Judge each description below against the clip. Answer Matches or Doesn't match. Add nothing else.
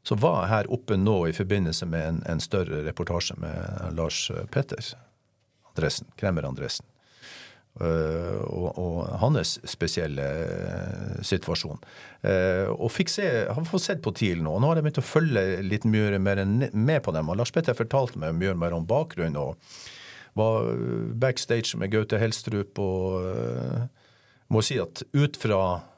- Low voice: Matches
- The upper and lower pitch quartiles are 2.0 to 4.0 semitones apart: Doesn't match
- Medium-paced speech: Doesn't match